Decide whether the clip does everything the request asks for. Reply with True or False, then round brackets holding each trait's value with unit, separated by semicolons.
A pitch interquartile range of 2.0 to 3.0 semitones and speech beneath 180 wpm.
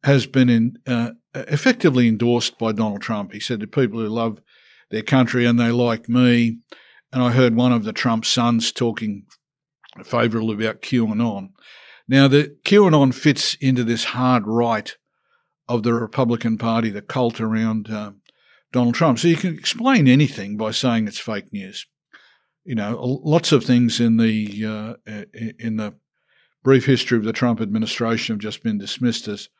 True (2.6 semitones; 165 wpm)